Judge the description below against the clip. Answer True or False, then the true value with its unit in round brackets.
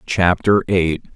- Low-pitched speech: True (90 Hz)